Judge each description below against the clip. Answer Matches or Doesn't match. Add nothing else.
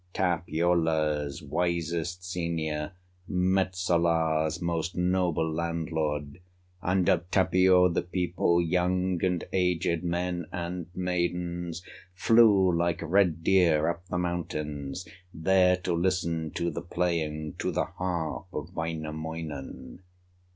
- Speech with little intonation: Matches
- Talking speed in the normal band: Doesn't match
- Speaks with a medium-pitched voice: Doesn't match